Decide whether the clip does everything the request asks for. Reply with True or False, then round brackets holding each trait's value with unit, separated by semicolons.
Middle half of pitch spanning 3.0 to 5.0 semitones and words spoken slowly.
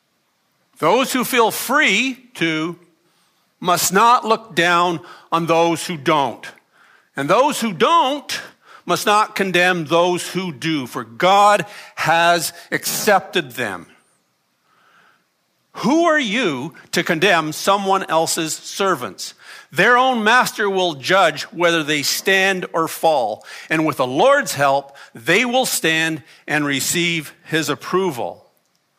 True (4.3 semitones; 120 wpm)